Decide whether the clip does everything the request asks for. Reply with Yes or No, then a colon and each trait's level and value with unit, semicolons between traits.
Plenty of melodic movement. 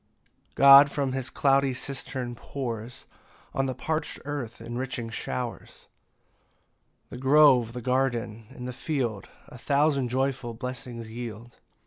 No: narrow, 2.5 semitones